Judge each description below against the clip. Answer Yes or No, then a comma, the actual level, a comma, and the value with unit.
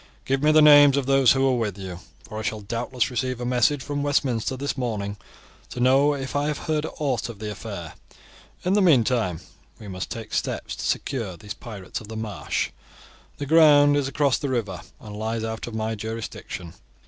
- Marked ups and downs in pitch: No, average, 4.7 semitones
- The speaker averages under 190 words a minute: No, average, 200 wpm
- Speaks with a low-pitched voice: Yes, low, 120 Hz